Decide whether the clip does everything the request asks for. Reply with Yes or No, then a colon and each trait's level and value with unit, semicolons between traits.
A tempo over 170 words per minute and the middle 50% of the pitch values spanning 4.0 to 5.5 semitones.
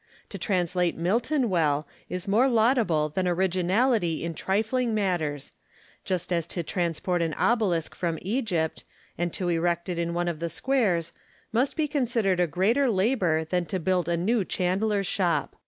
No: average, 160 wpm; average, 4.4 semitones